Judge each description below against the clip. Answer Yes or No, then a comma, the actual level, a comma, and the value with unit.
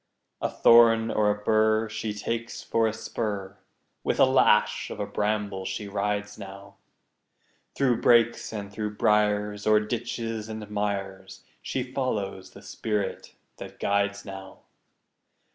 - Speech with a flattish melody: Yes, narrow, 1.7 semitones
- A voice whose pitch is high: No, low, 105 Hz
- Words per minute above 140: No, slow, 135 wpm